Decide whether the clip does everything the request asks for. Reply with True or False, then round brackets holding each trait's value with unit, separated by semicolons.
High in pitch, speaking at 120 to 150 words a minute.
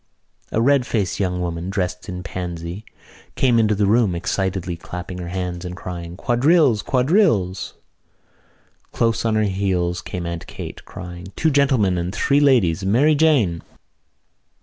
False (95 Hz; 145 wpm)